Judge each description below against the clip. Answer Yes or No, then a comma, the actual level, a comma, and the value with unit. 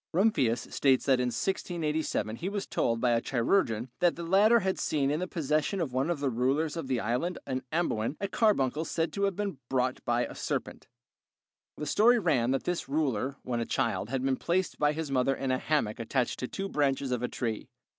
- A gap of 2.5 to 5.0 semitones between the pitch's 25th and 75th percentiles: No, wide, 5.4 semitones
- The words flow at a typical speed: No, fast, 215 wpm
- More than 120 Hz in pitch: Yes, medium, 140 Hz